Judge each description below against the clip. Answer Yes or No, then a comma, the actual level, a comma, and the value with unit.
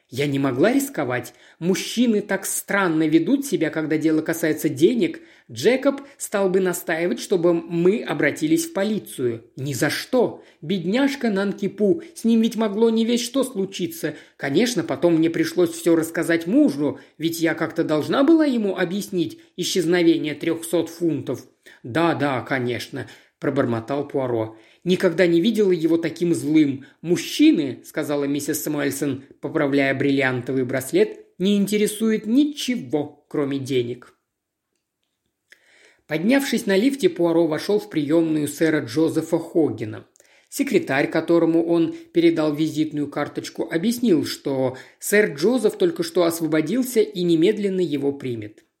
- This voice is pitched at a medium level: Yes, medium, 170 Hz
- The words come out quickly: No, average, 125 wpm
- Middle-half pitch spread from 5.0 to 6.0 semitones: Yes, wide, 5.5 semitones